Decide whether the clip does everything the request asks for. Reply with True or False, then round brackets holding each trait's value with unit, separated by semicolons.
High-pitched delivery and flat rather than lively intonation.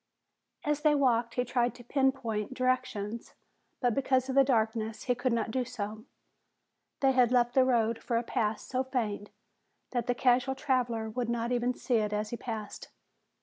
True (245 Hz; 2.3 semitones)